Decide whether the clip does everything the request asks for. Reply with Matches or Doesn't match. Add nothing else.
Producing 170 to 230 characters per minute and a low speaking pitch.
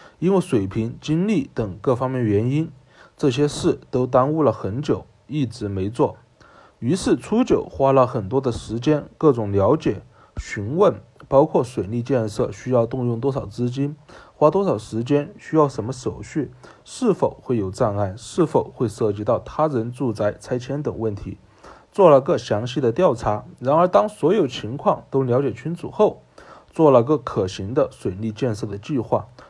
Doesn't match